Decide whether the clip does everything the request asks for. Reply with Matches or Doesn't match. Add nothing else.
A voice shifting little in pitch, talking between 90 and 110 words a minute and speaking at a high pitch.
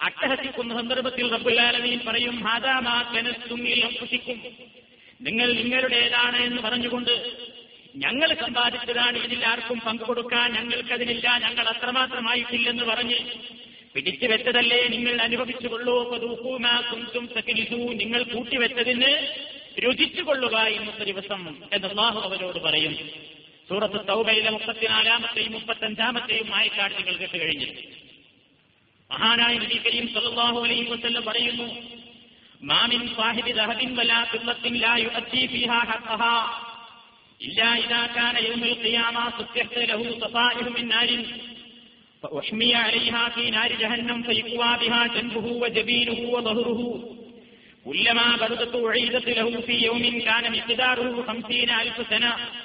Matches